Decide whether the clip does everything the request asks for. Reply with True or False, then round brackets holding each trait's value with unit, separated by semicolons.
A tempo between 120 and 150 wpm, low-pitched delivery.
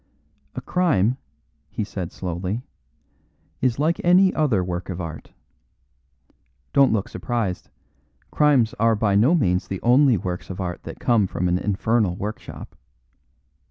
True (135 wpm; 105 Hz)